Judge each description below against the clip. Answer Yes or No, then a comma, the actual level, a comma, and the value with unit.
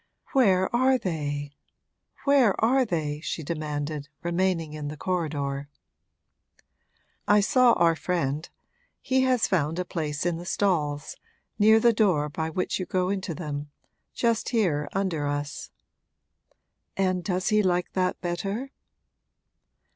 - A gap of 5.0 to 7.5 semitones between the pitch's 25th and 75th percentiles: Yes, average, 5.3 semitones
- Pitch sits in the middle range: Yes, medium, 175 Hz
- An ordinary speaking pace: No, slow, 130 wpm